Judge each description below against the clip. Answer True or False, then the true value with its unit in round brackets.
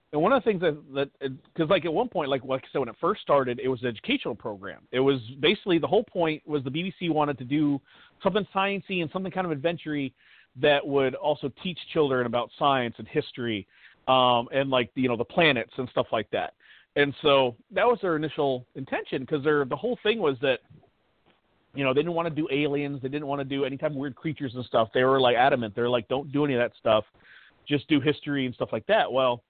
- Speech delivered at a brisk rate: True (240 wpm)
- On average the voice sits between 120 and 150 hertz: True (140 Hz)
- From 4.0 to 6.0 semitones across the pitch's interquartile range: False (3.3 semitones)